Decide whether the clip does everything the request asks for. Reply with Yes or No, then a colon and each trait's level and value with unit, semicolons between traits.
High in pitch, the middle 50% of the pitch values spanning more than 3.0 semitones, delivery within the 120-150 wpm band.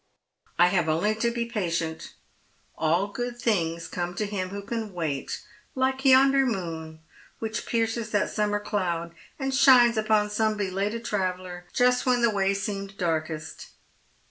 Yes: high, 205 Hz; average, 4.8 semitones; average, 145 wpm